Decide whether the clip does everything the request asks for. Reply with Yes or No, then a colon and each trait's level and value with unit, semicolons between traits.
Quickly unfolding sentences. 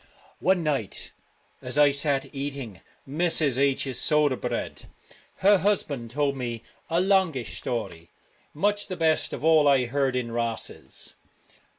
No: average, 140 wpm